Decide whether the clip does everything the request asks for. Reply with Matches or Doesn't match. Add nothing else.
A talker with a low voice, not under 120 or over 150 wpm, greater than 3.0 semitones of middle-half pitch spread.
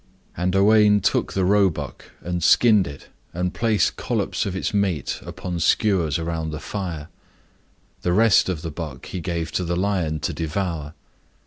Doesn't match